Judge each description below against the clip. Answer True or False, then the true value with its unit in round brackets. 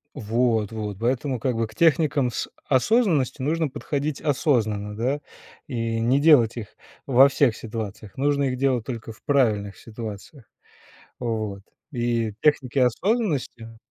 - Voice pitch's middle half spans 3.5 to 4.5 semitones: True (4.0 semitones)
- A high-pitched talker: False (125 Hz)